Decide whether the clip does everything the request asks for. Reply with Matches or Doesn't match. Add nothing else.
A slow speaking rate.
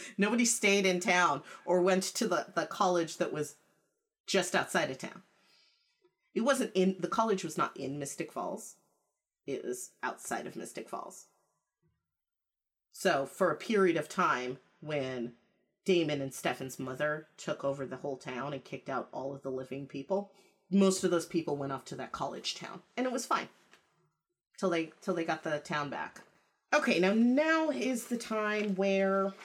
Doesn't match